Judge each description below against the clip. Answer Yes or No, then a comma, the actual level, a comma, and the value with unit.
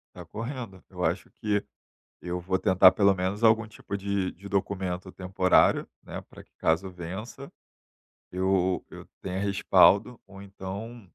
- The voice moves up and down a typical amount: No, narrow, 1.8 semitones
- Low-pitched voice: Yes, very low, 95 Hz